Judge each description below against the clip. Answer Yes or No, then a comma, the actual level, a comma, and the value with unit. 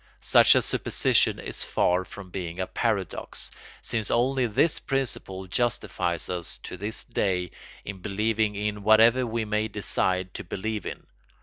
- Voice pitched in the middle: No, low, 105 Hz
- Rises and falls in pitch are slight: No, average, 3.2 semitones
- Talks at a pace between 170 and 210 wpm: No, average, 145 wpm